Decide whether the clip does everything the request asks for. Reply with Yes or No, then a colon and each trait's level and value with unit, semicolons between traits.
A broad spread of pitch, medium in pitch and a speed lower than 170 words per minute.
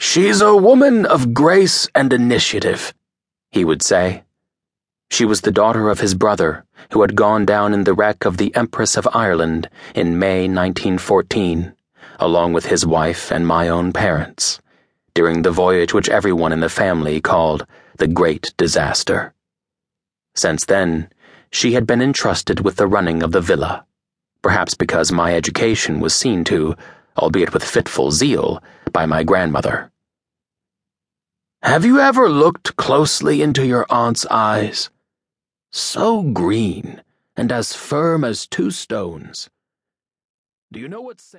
No: wide, 7.1 semitones; low, 100 Hz; average, 145 wpm